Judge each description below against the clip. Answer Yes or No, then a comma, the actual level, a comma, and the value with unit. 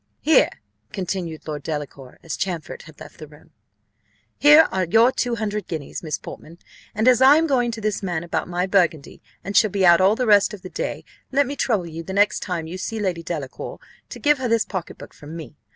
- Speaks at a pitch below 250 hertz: Yes, high, 190 Hz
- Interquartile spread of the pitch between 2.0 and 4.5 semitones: No, wide, 5.4 semitones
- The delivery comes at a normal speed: No, fast, 220 wpm